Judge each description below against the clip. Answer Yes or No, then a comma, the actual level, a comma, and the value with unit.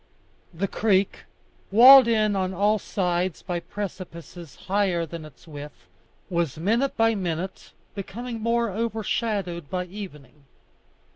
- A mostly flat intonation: No, average, 4.0 semitones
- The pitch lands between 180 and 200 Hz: Yes, high, 190 Hz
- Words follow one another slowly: Yes, slow, 120 wpm